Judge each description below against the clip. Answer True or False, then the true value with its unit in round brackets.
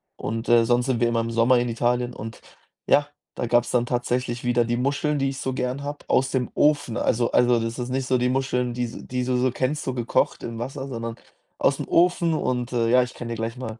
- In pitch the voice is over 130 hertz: False (125 Hz)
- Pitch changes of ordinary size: False (1.7 semitones)